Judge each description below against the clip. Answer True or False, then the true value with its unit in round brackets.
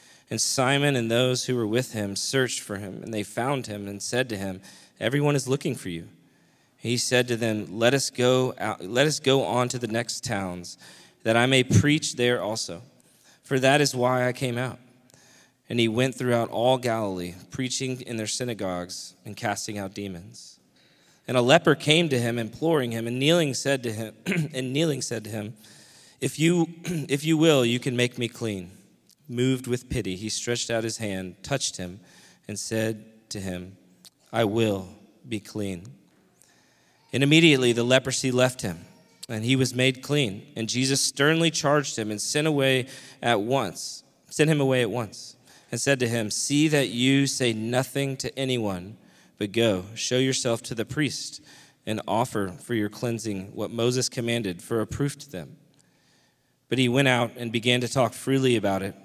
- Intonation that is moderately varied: True (3.4 semitones)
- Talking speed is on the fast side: False (185 wpm)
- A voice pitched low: True (125 Hz)